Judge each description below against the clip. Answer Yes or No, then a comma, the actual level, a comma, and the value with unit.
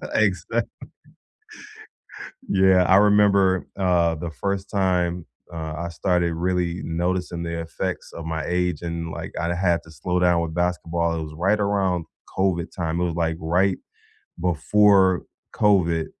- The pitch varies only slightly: Yes, narrow, 2.0 semitones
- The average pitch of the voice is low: Yes, very low, 90 Hz